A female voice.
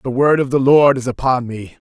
No: male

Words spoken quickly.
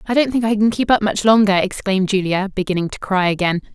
Yes: fast, 240 wpm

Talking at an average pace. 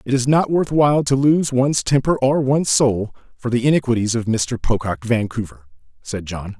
Yes: average, 190 wpm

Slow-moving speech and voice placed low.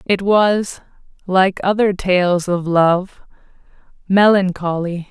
No: slow, 95 wpm; medium, 185 Hz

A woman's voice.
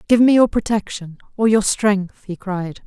Yes: female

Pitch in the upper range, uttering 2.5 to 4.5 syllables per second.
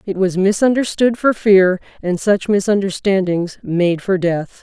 Yes: high, 195 Hz; 4.2 syllables/s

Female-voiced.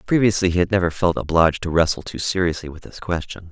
No: male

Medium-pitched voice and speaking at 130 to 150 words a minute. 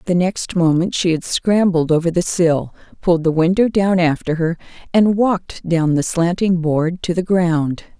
No: medium, 175 Hz; average, 180 wpm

